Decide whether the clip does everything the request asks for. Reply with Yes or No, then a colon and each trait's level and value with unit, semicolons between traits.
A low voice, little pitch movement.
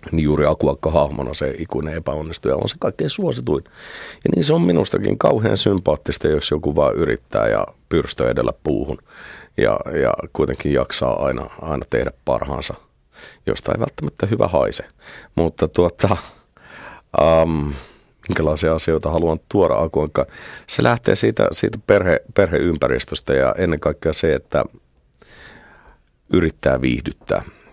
Yes: very low, 80 Hz; narrow, 1.9 semitones